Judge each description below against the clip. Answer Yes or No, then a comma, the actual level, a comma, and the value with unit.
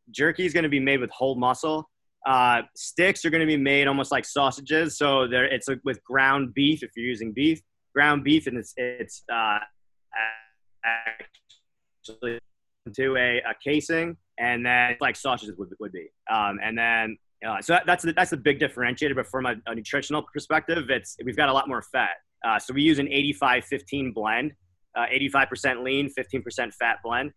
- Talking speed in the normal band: Yes, average, 185 wpm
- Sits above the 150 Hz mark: No, low, 135 Hz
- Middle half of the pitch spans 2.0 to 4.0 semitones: Yes, average, 3.7 semitones